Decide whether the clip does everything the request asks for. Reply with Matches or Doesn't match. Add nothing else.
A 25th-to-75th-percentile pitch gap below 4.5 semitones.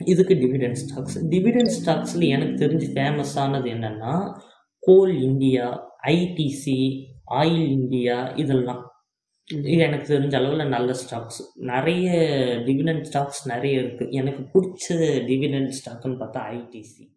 Matches